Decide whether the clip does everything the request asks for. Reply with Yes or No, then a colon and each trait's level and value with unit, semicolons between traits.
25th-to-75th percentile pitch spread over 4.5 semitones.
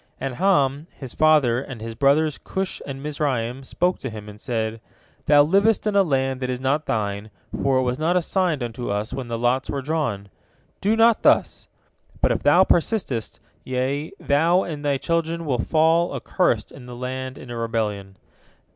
Yes: average, 5.0 semitones